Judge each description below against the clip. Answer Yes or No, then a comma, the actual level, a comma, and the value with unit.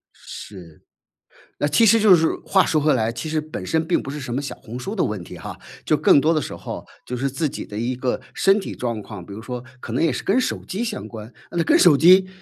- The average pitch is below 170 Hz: Yes, medium, 140 Hz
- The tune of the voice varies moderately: No, wide, 6.8 semitones